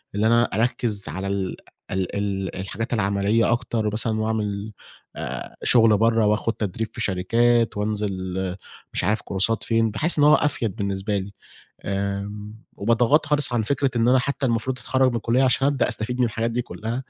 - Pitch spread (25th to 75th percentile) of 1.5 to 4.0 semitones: Yes, average, 3.0 semitones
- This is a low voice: Yes, low, 110 Hz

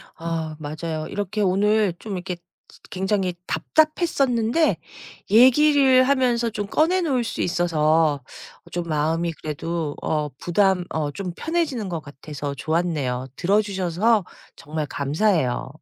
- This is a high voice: No, medium, 180 Hz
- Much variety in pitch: Yes, wide, 6.3 semitones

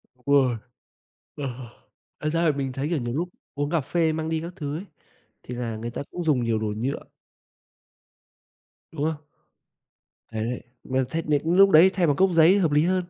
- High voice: No, medium, 150 Hz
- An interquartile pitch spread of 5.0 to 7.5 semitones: No, average, 4.5 semitones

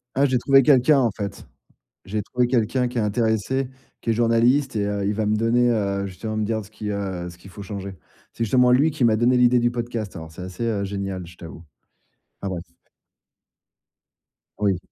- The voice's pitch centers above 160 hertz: No, low, 110 Hz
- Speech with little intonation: No, average, 3.6 semitones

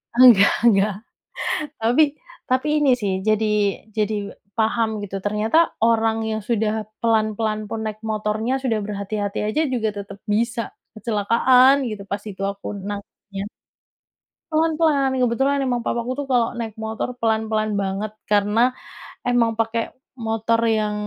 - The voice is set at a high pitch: Yes, high, 220 Hz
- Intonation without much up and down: Yes, narrow, 2.3 semitones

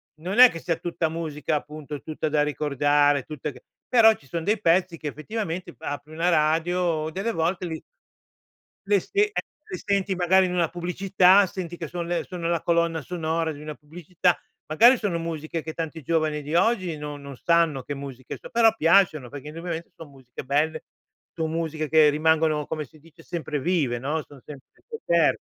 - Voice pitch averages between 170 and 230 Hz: No, medium, 160 Hz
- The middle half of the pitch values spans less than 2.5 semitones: No, average, 2.8 semitones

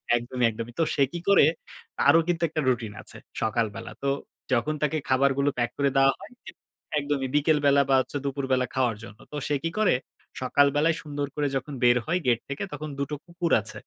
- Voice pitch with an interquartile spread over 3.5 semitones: No, average, 2.9 semitones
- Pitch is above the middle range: No, medium, 140 Hz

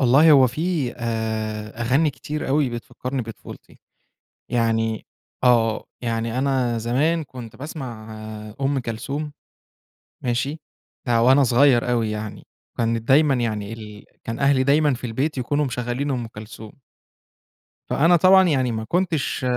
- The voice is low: Yes, low, 125 Hz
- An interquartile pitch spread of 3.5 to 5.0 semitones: Yes, average, 3.8 semitones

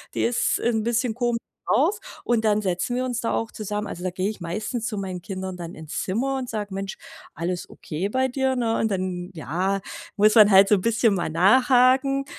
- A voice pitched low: No, high, 215 Hz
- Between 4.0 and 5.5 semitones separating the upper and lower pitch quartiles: Yes, average, 4.5 semitones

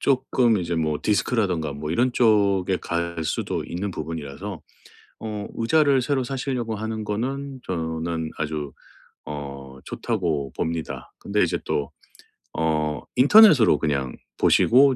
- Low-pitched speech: Yes, very low, 95 Hz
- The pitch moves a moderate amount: No, wide, 7.3 semitones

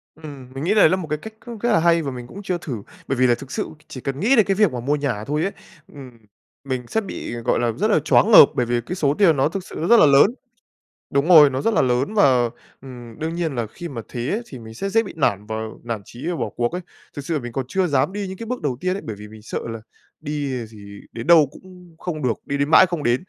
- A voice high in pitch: No, medium, 145 Hz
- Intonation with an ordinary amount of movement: No, wide, 6.6 semitones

